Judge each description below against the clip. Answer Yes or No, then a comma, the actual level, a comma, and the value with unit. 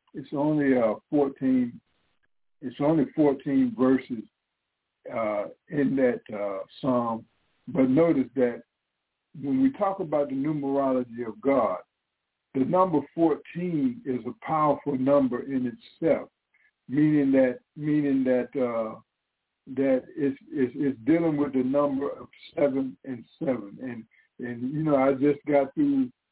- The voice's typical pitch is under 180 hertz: Yes, low, 135 Hz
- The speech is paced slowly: Yes, slow, 130 wpm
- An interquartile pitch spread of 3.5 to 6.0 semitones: No, average, 2.7 semitones